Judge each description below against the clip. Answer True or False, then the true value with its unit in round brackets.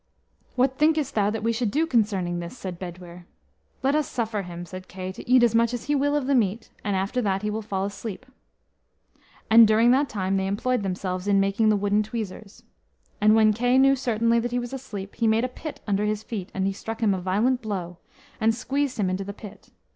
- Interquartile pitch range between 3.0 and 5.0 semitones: True (3.9 semitones)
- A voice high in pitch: True (215 Hz)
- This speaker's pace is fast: True (225 wpm)